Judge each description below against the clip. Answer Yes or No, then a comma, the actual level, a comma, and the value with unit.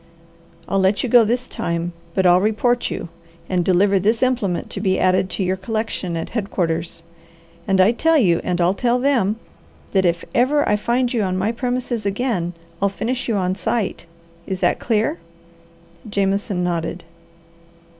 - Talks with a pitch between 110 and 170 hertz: No, high, 200 Hz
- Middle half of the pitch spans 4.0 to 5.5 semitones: Yes, average, 4.5 semitones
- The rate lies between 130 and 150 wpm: No, average, 165 wpm